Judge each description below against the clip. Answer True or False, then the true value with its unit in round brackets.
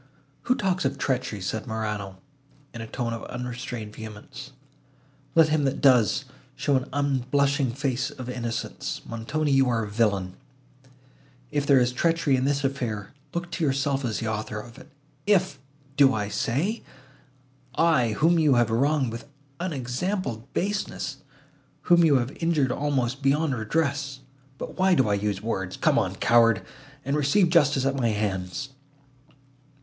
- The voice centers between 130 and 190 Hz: True (135 Hz)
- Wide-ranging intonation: False (4.1 semitones)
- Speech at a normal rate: True (145 wpm)